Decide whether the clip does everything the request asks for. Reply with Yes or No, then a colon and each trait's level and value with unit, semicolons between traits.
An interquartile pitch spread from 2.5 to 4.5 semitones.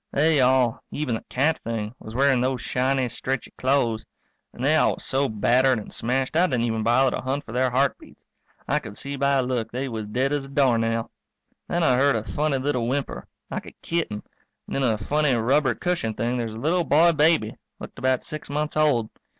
Yes: average, 3.5 semitones